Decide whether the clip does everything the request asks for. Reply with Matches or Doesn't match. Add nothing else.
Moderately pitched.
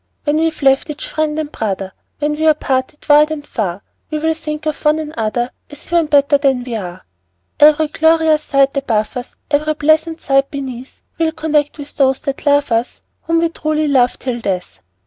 Doesn't match